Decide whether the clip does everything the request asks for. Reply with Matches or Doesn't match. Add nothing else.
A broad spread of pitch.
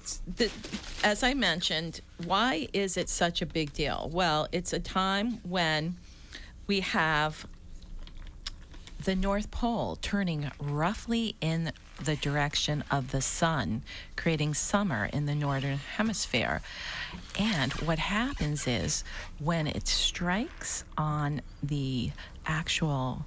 Matches